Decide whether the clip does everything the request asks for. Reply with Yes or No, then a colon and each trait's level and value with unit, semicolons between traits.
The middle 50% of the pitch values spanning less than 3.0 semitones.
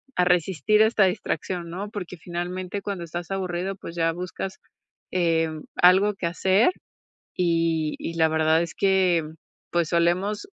Yes: narrow, 2.4 semitones